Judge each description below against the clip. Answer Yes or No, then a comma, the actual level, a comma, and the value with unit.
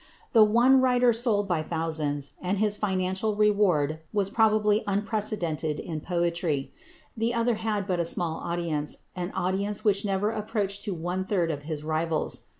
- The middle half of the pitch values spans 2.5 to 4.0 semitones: No, average, 4.4 semitones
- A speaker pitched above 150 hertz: Yes, high, 190 Hz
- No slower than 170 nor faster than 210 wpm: No, average, 155 wpm